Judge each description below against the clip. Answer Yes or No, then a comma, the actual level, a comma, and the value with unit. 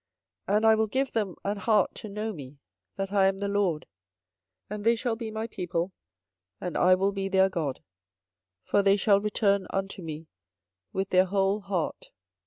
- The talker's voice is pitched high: Yes, high, 195 Hz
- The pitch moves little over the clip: Yes, narrow, 2.1 semitones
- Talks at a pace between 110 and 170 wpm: No, average, 185 wpm